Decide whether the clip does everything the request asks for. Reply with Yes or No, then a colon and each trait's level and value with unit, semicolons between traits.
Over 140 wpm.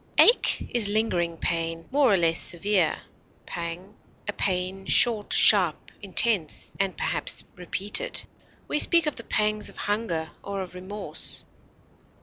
No: slow, 135 wpm